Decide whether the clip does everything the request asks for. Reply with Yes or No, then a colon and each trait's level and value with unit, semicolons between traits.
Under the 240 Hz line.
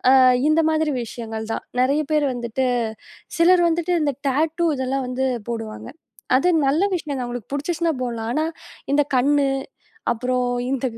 No: very high, 275 Hz